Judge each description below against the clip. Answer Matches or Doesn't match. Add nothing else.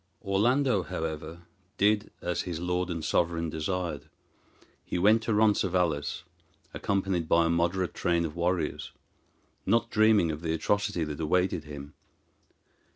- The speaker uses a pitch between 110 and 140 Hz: Doesn't match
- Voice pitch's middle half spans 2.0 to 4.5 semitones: Matches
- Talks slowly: Matches